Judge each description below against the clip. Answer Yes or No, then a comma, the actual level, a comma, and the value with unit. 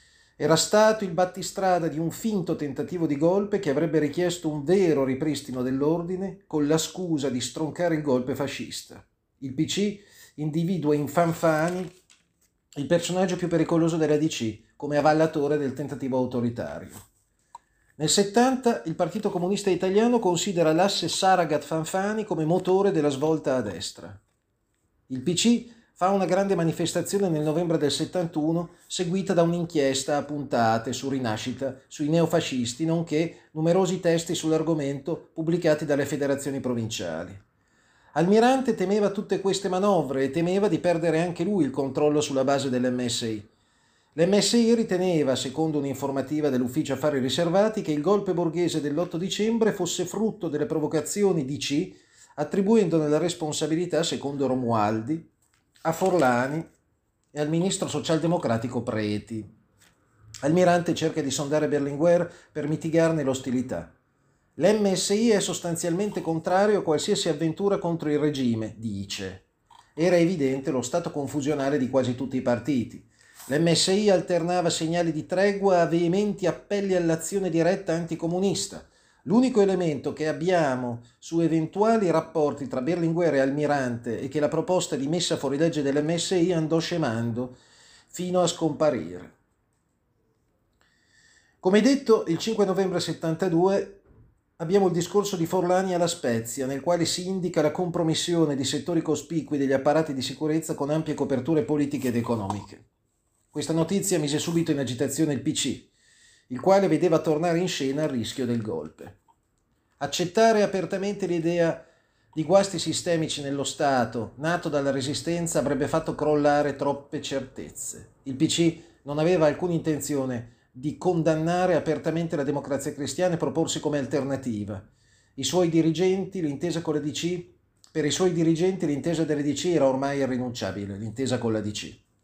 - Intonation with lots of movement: No, average, 4.3 semitones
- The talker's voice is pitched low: No, medium, 160 Hz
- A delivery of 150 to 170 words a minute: No, average, 135 wpm